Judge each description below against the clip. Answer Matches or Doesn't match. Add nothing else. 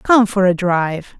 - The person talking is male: Doesn't match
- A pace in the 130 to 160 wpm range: Doesn't match